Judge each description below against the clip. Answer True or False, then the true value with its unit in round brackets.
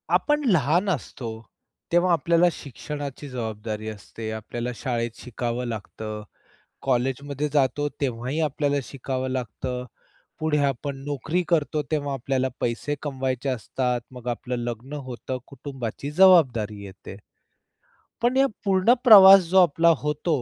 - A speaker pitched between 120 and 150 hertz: True (135 Hz)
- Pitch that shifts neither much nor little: True (4.1 semitones)